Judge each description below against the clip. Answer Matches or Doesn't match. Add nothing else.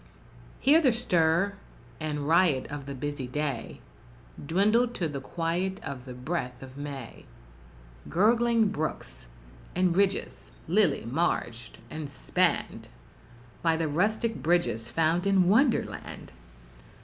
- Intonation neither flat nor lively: Doesn't match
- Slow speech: Matches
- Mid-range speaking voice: Matches